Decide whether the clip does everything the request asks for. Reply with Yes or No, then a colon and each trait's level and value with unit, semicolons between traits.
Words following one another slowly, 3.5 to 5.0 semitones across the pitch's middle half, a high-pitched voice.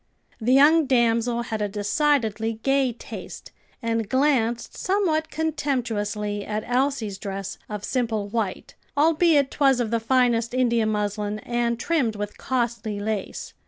Yes: slow, 130 wpm; average, 4.1 semitones; high, 235 Hz